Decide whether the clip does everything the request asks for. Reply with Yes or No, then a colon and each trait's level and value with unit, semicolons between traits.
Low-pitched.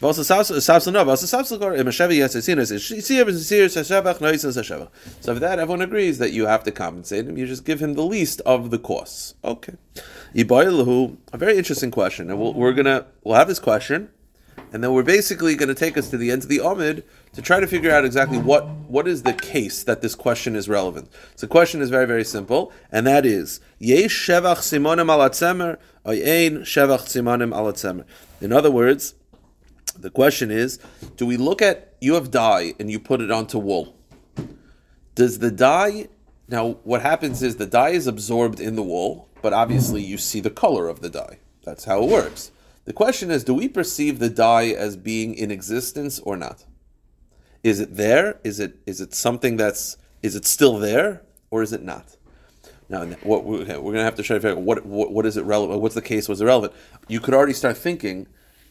Yes: low, 125 Hz